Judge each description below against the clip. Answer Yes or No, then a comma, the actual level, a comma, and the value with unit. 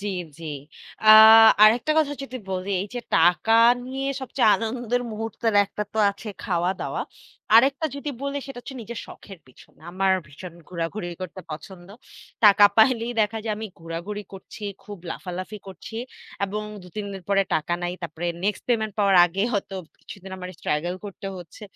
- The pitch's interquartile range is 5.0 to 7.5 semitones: No, average, 3.7 semitones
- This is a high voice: Yes, high, 205 Hz